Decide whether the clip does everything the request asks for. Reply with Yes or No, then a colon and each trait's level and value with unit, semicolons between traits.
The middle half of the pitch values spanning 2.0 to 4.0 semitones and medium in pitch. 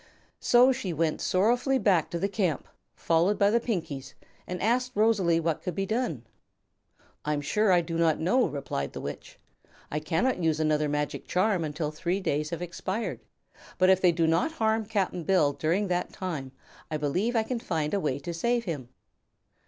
No: wide, 5.4 semitones; medium, 175 Hz